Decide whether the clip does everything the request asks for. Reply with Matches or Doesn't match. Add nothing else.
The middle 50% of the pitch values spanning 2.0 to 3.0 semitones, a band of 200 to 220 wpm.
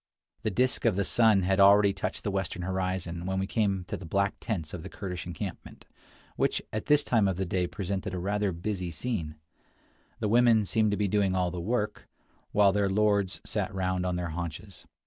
Matches